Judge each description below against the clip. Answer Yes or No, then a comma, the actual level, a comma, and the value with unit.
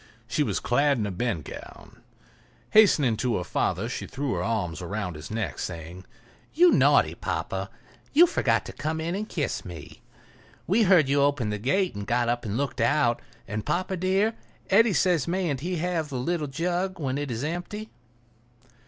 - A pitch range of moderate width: No, wide, 8.0 semitones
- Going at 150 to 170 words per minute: No, average, 180 wpm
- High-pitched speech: No, medium, 140 Hz